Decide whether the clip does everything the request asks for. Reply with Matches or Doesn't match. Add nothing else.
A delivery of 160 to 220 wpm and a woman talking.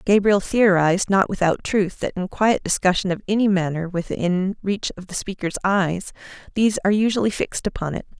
Matches